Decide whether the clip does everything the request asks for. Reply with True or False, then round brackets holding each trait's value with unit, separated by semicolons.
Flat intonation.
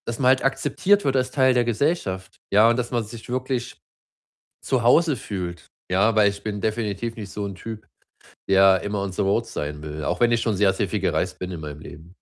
False (4.3 semitones)